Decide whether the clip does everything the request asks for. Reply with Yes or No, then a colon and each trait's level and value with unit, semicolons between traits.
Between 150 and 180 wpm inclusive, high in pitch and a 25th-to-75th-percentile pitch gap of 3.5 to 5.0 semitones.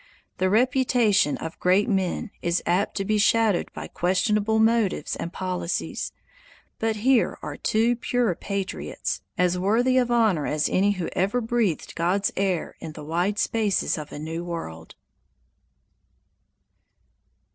No: slow, 135 wpm; high, 195 Hz; average, 4.2 semitones